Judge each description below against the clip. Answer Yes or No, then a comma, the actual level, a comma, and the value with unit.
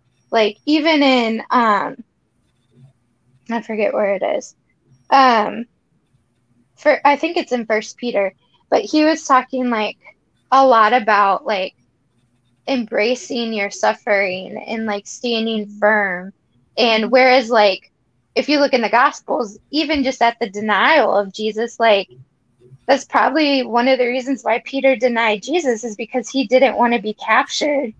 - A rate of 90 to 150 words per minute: Yes, average, 145 wpm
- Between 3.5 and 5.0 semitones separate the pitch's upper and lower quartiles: Yes, average, 4.5 semitones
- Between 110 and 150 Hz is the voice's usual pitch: No, high, 225 Hz